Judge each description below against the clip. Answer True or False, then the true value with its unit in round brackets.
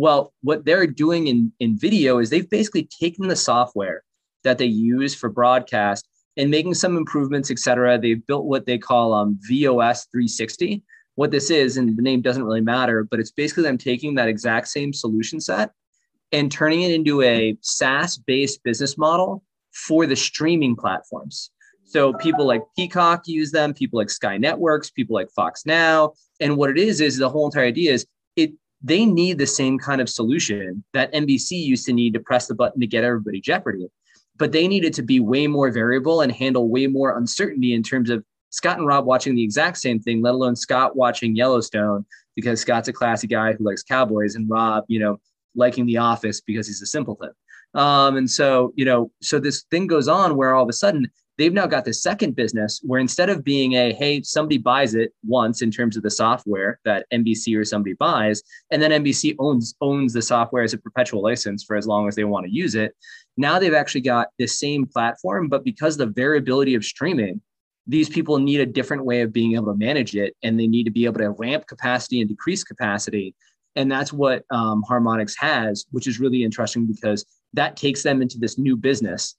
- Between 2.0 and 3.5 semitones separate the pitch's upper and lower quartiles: False (4.3 semitones)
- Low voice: True (125 Hz)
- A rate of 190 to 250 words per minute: True (205 wpm)